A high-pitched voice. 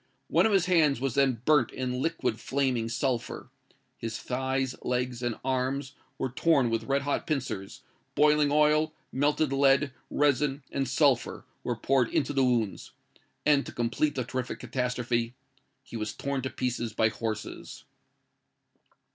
No: low, 130 Hz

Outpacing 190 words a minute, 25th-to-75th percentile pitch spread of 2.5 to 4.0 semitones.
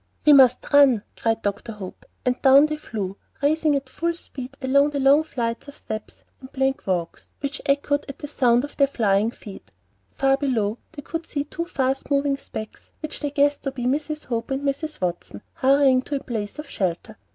Yes: average, 200 wpm; average, 3.7 semitones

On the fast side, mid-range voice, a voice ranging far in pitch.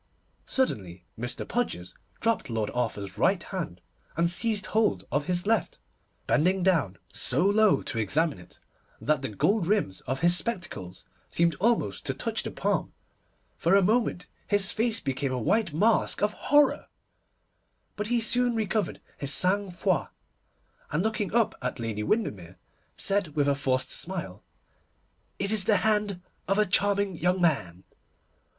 No: average, 150 wpm; medium, 180 Hz; wide, 8.3 semitones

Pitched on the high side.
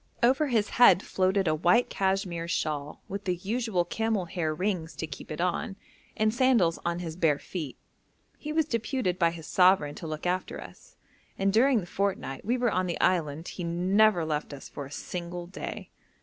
No: medium, 180 Hz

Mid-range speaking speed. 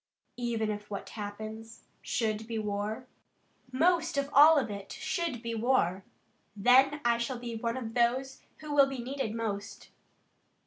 Yes: average, 150 wpm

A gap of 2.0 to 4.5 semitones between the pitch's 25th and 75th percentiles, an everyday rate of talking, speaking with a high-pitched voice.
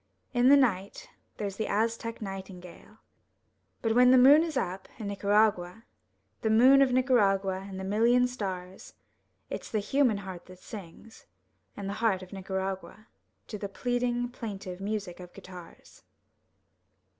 Yes: average, 4.1 semitones; average, 145 wpm; high, 205 Hz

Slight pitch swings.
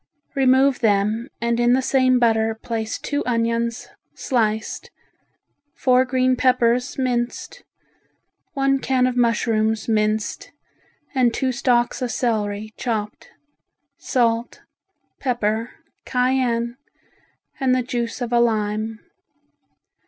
Yes: narrow, 2.3 semitones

